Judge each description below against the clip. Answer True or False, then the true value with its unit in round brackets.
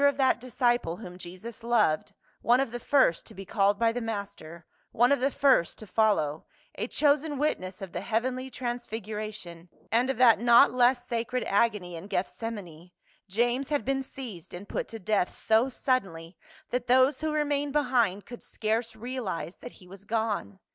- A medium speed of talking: True (175 wpm)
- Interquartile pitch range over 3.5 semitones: True (4.5 semitones)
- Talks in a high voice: True (230 Hz)